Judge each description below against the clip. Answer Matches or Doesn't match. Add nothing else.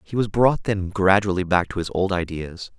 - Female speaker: Doesn't match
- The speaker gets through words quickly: Matches